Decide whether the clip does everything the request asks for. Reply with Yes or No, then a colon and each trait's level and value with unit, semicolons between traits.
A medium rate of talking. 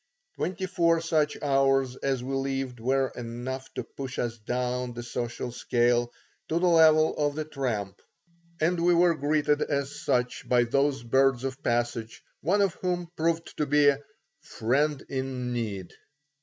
Yes: average, 155 wpm